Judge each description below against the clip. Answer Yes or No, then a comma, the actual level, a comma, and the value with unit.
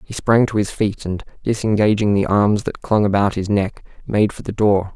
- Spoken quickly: Yes, fast, 220 wpm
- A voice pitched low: Yes, low, 105 Hz